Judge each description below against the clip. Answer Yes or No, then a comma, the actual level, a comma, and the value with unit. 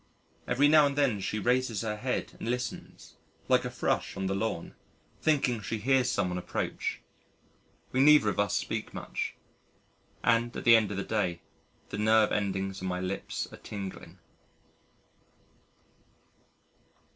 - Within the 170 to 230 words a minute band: No, average, 145 wpm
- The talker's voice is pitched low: Yes, low, 110 Hz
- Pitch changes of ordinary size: Yes, average, 4.2 semitones